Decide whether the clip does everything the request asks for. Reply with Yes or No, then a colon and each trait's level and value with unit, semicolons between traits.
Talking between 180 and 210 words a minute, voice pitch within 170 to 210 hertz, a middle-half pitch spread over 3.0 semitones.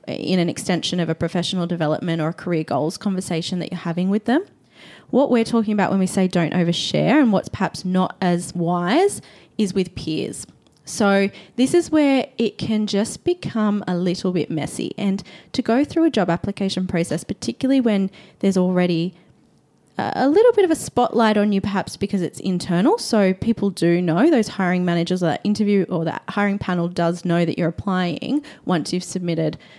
Yes: average, 185 wpm; medium, 185 Hz; average, 3.6 semitones